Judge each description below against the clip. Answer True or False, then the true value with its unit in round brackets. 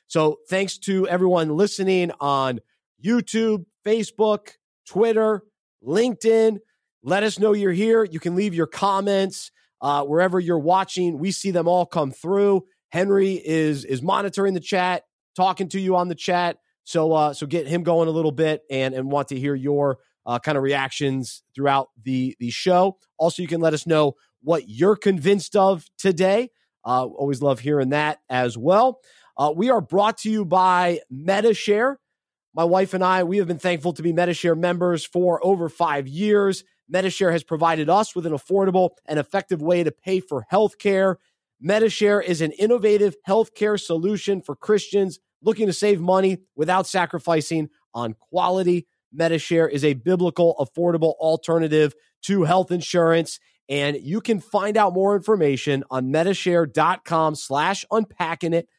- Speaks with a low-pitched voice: False (180 Hz)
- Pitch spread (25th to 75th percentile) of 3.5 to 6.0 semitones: True (4.0 semitones)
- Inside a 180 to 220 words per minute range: False (165 wpm)